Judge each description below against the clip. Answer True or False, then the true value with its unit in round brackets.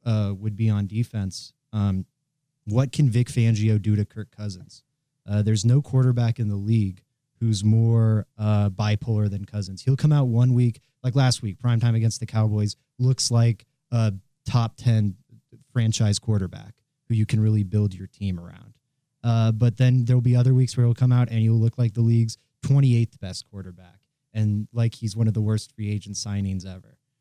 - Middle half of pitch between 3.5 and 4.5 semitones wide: False (3.1 semitones)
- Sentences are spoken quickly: False (185 wpm)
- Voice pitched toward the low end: True (115 Hz)